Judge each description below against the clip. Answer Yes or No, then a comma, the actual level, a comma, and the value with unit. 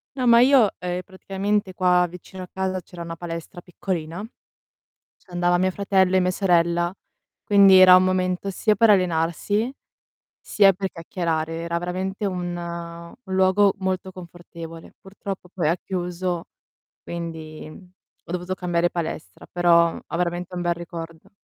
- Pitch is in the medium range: Yes, medium, 180 Hz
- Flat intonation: Yes, narrow, 1.9 semitones